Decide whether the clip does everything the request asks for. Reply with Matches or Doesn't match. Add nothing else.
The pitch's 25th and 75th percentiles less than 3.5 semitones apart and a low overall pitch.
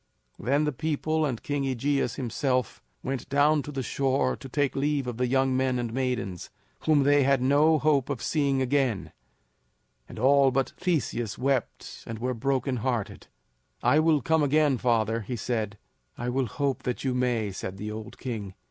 Matches